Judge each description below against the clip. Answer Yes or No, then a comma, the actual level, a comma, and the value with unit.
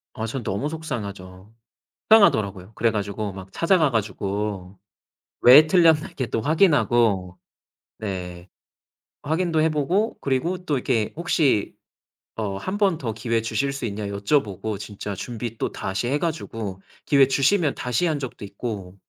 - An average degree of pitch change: No, wide, 7.0 semitones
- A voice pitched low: Yes, low, 115 Hz